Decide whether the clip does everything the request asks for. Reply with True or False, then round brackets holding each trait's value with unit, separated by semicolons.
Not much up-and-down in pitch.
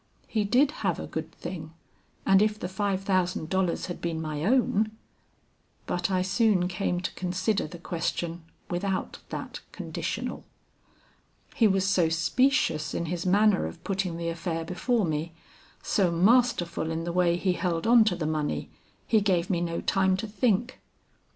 False (3.2 semitones)